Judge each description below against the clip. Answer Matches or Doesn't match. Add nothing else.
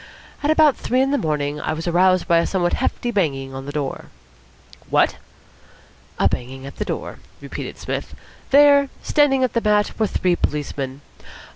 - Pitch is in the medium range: Matches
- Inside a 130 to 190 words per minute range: Matches